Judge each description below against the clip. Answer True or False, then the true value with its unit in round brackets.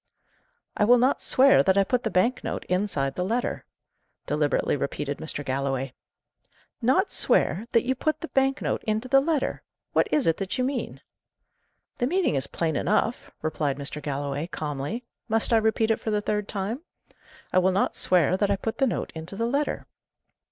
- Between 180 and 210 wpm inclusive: True (185 wpm)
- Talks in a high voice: True (210 Hz)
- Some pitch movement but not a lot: False (8.2 semitones)